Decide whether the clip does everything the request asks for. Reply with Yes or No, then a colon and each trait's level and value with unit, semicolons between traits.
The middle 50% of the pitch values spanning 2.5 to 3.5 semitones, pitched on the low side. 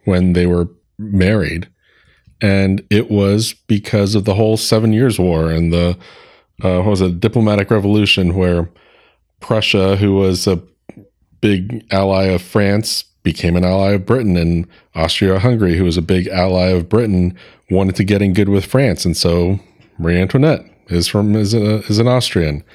Yes: average, 3.0 semitones; very low, 95 Hz